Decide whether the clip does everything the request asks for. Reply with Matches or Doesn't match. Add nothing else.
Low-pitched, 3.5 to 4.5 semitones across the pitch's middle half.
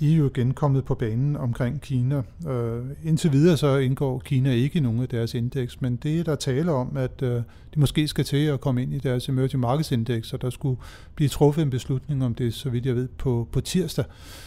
Doesn't match